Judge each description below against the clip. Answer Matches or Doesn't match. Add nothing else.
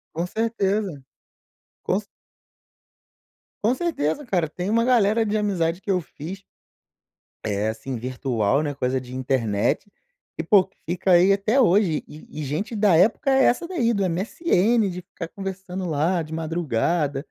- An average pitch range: Doesn't match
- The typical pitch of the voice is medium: Matches